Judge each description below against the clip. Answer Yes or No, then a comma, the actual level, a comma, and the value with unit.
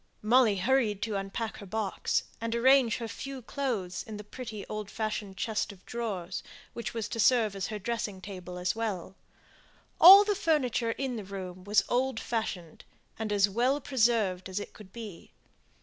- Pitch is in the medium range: No, high, 215 Hz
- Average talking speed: Yes, average, 180 wpm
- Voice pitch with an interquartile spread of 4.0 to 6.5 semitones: No, average, 3.3 semitones